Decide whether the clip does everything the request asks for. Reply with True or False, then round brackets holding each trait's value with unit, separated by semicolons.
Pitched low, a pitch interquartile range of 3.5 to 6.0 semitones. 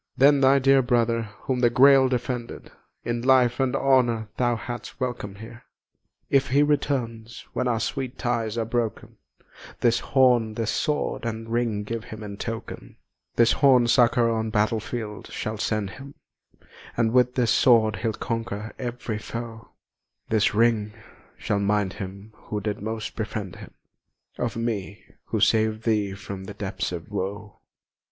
False (115 Hz; 2.4 semitones)